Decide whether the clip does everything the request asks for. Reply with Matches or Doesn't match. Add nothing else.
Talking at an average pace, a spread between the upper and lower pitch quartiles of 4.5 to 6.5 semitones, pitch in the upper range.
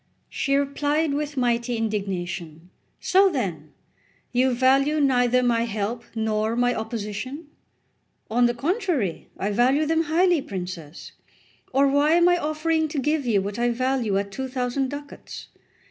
Matches